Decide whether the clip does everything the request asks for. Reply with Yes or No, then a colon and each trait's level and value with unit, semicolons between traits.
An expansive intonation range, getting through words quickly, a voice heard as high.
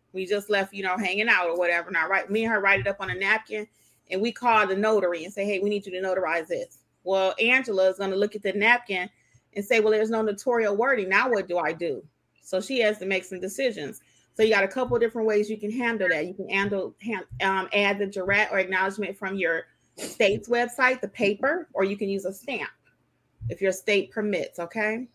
No: narrow, 2.5 semitones; fast, 240 wpm; high, 200 Hz